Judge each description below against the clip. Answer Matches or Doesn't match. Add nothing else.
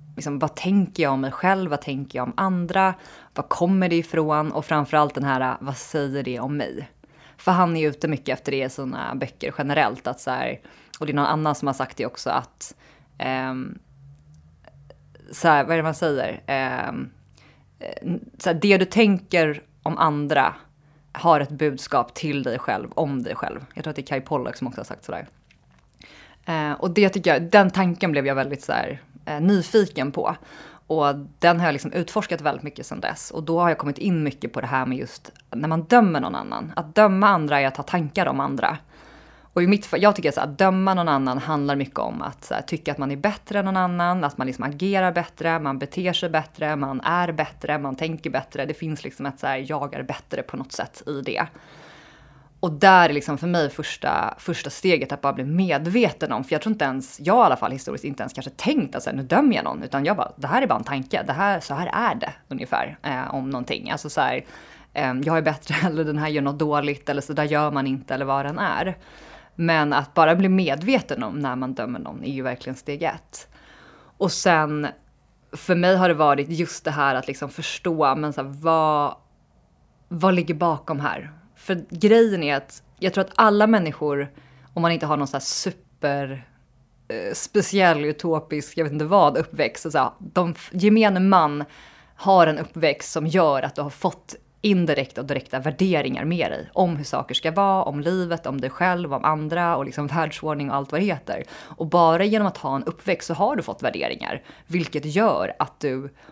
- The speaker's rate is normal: Doesn't match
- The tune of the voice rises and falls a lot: Doesn't match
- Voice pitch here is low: Doesn't match